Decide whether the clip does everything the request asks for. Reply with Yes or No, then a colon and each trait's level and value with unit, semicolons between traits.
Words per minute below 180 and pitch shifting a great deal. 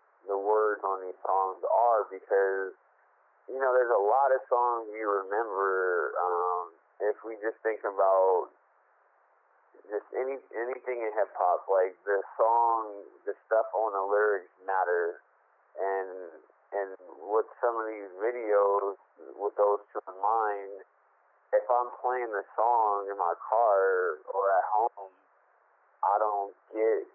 No: average, 140 wpm; average, 3.3 semitones